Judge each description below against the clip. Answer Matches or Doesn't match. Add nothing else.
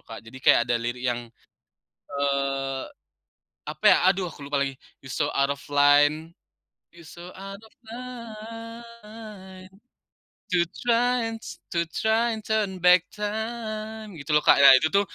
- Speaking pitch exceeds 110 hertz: Matches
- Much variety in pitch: Matches